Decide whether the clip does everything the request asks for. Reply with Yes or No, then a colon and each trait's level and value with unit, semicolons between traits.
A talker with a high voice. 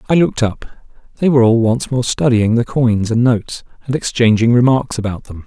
No: low, 120 Hz